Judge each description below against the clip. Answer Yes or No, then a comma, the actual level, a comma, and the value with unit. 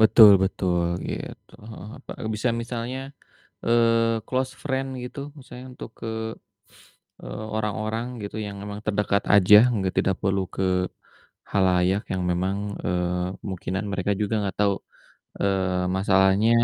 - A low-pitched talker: Yes, low, 105 Hz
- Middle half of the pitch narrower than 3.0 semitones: No, average, 3.4 semitones